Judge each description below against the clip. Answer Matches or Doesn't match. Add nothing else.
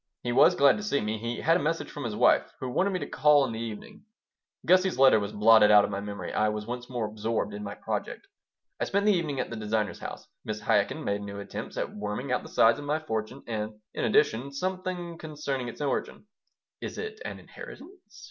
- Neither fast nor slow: Doesn't match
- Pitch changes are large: Matches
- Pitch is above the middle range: Doesn't match